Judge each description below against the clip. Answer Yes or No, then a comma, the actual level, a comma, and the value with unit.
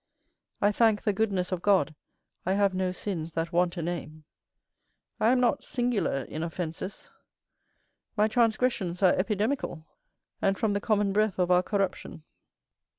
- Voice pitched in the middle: No, high, 195 Hz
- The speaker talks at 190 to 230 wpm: No, average, 150 wpm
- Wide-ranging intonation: No, average, 3.5 semitones